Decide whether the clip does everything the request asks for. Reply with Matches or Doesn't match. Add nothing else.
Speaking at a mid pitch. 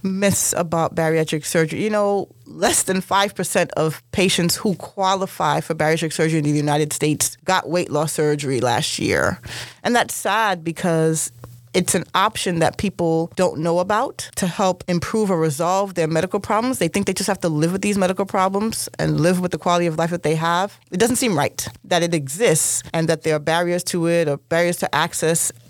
Matches